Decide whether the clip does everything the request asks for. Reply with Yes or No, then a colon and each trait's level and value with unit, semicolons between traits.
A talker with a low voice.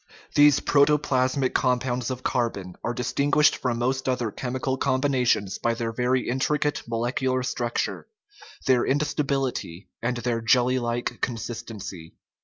Yes: low, 125 Hz